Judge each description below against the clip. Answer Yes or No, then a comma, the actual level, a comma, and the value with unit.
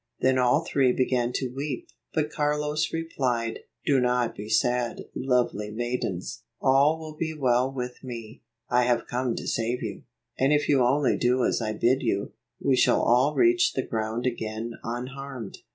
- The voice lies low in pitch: Yes, low, 125 Hz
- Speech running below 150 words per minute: No, average, 170 wpm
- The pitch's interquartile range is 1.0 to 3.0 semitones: Yes, average, 2.7 semitones